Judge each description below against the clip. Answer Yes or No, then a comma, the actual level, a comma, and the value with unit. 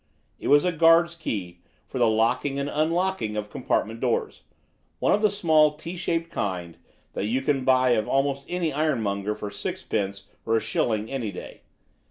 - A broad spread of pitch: Yes, wide, 6.9 semitones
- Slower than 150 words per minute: No, average, 180 wpm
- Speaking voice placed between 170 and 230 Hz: No, low, 135 Hz